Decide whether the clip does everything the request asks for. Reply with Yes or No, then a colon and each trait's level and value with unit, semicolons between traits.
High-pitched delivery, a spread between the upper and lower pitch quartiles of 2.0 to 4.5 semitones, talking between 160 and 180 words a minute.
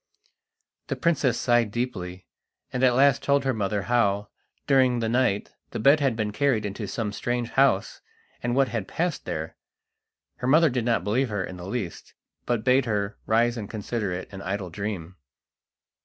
No: low, 115 Hz; average, 4.1 semitones; average, 175 wpm